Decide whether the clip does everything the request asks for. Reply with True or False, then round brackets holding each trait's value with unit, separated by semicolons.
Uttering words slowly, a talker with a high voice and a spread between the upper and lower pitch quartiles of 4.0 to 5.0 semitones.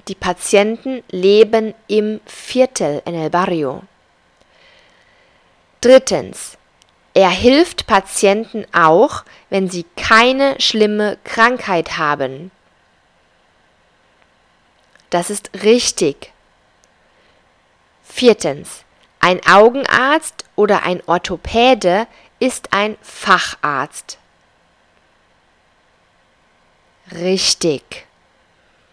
True (65 wpm; 200 Hz; 4.7 semitones)